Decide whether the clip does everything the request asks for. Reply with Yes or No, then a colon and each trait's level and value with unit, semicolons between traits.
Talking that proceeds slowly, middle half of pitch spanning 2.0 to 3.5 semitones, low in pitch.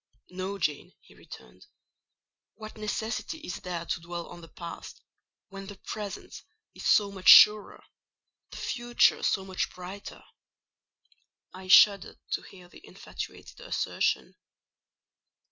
No: slow, 120 wpm; average, 2.8 semitones; high, 195 Hz